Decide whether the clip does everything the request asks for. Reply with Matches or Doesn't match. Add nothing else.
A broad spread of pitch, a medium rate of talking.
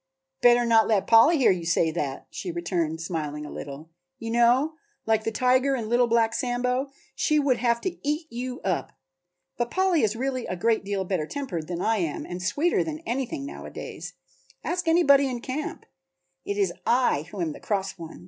Matches